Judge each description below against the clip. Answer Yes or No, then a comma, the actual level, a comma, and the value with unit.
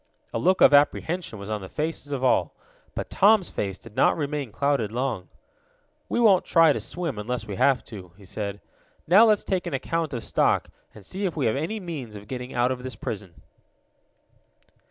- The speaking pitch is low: Yes, low, 130 Hz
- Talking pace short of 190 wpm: No, average, 195 wpm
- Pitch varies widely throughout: Yes, wide, 7.6 semitones